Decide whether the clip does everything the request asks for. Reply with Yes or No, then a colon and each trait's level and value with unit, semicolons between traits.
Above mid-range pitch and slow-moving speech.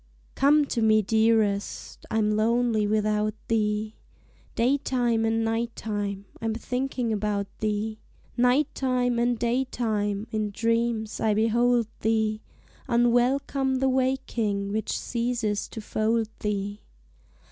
Yes: high, 225 Hz; slow, 115 wpm